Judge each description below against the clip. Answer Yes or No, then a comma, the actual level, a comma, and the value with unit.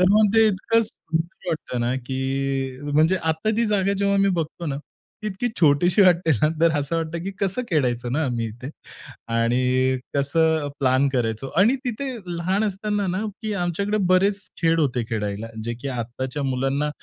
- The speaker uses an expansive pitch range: Yes, wide, 7.0 semitones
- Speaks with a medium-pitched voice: Yes, medium, 160 Hz